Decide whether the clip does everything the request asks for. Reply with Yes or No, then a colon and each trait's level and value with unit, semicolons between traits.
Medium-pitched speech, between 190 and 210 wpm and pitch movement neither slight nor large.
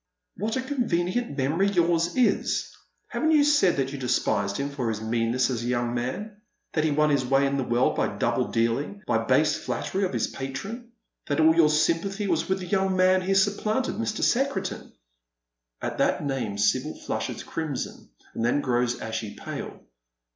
No: medium, 150 Hz; average, 195 wpm; wide, 7.8 semitones